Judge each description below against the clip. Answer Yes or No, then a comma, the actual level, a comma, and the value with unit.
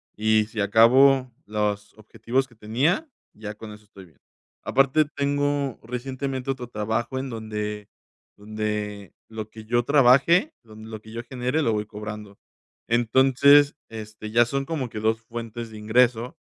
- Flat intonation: No, average, 3.7 semitones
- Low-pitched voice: Yes, low, 115 Hz